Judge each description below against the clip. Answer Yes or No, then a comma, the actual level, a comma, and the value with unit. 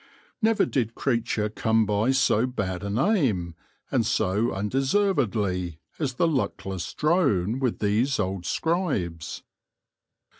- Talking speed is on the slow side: Yes, slow, 120 wpm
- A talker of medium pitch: No, low, 115 Hz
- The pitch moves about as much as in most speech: No, wide, 5.8 semitones